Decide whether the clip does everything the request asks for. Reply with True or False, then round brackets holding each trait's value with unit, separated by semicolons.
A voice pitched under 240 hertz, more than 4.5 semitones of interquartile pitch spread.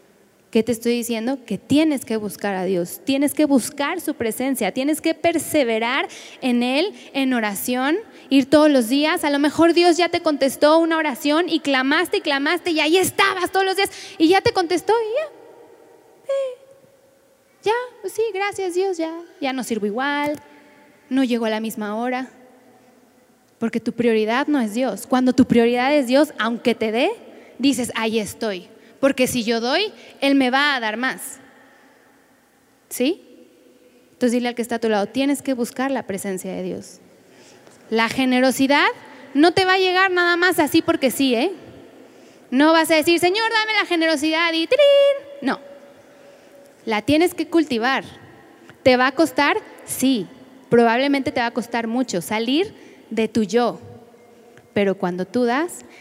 False (275 Hz; 5.3 semitones)